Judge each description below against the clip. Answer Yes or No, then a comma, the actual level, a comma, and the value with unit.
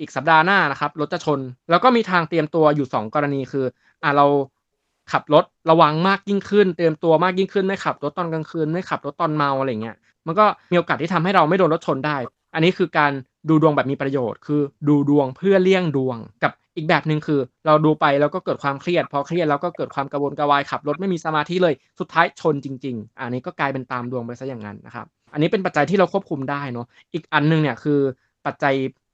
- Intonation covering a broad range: No, average, 3.5 semitones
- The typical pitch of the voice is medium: Yes, medium, 150 Hz